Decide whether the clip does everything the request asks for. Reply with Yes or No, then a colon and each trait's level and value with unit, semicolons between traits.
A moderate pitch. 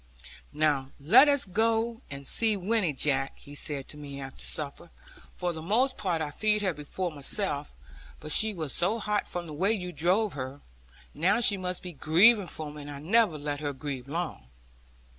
Yes: medium, 170 Hz